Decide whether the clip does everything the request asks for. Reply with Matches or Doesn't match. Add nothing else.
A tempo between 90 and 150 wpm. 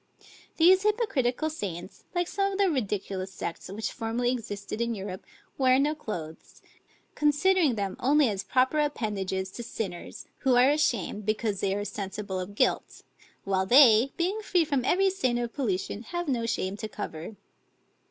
Doesn't match